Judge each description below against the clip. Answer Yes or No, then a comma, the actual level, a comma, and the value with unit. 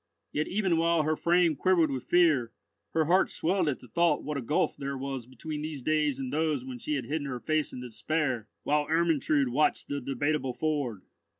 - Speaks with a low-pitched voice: No, medium, 150 Hz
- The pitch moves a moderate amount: Yes, average, 3.4 semitones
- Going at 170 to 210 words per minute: Yes, average, 200 wpm